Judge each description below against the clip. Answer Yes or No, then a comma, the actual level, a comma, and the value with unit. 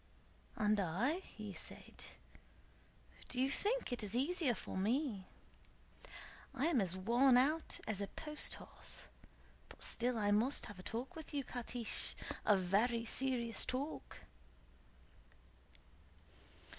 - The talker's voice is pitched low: No, high, 240 Hz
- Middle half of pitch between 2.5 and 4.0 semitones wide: No, average, 4.8 semitones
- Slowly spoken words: Yes, slow, 125 wpm